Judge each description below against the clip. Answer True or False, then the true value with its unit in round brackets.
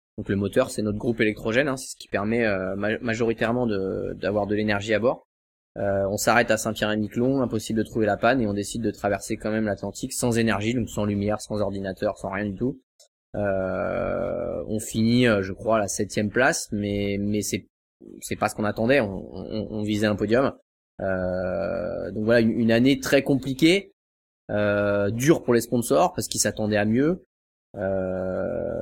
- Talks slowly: False (190 wpm)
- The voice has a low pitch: True (105 Hz)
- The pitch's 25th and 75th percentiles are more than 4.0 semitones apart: False (2.7 semitones)